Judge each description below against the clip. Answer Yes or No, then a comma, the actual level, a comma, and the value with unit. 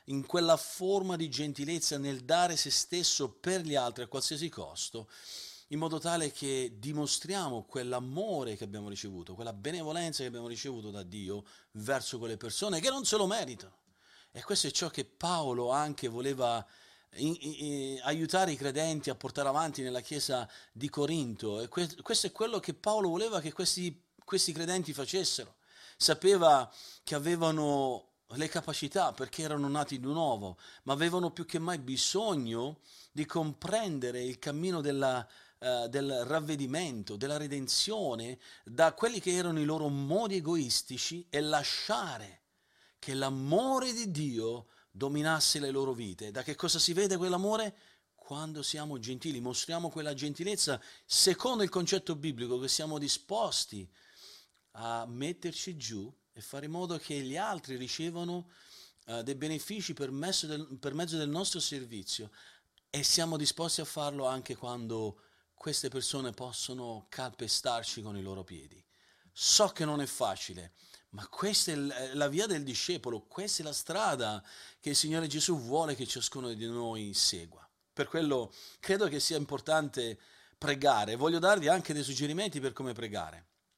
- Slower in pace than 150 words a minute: No, average, 155 wpm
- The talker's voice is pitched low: No, medium, 145 Hz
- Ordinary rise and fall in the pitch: Yes, average, 5.0 semitones